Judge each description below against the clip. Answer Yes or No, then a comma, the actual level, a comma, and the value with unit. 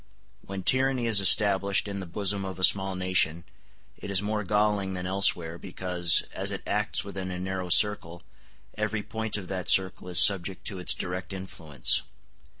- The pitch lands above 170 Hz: No, very low, 95 Hz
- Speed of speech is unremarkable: Yes, average, 170 wpm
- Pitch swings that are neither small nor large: No, narrow, 2.0 semitones